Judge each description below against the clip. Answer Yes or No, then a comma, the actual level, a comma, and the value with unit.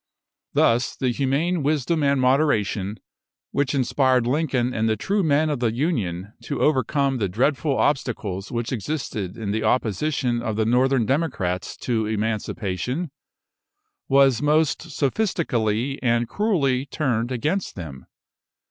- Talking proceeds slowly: Yes, slow, 130 wpm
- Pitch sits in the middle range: No, low, 130 Hz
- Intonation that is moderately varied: Yes, average, 4.6 semitones